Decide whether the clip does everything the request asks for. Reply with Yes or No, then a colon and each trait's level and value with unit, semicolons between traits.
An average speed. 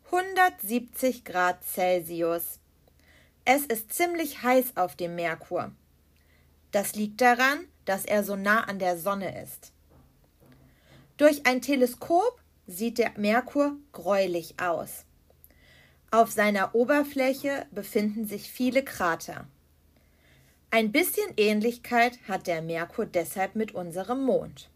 No: slow, 110 wpm